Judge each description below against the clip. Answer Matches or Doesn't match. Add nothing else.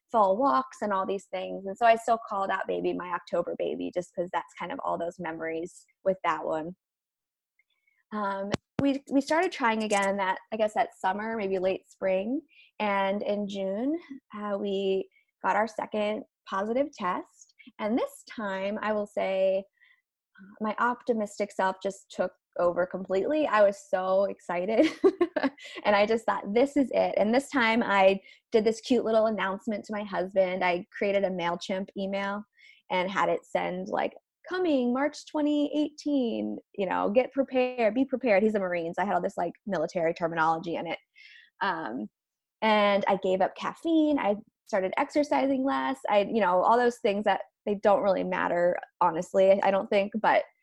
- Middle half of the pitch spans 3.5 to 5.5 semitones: Matches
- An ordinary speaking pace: Matches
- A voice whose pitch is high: Matches